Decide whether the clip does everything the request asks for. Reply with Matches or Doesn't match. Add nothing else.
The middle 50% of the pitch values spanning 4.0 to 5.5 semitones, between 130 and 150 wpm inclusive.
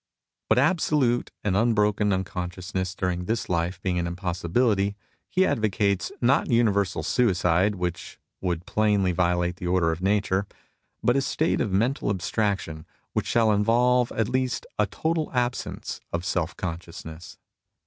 Matches